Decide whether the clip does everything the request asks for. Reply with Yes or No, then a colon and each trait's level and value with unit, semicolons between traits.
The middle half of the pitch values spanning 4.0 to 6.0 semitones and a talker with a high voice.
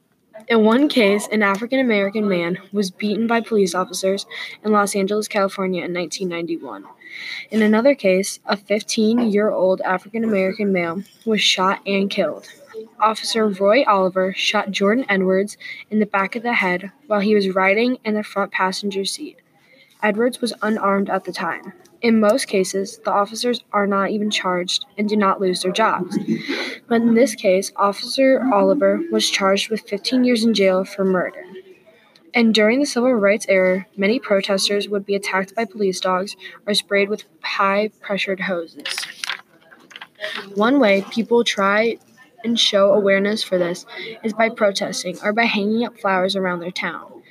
No: narrow, 2.5 semitones; high, 200 Hz